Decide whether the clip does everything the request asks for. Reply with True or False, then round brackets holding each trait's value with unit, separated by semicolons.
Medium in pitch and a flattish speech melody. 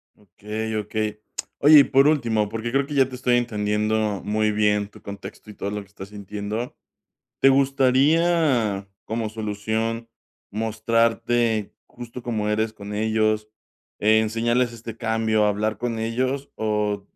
False (110 Hz; 2.2 semitones)